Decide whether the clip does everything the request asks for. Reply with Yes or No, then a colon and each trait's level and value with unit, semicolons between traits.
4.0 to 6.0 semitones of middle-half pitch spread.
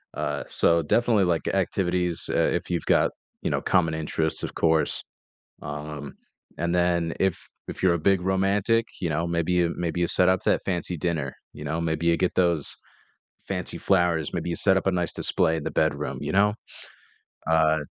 No: narrow, 2.5 semitones